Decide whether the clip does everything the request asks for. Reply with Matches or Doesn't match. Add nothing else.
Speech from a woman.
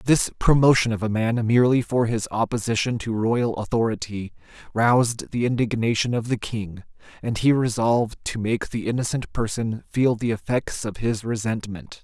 Doesn't match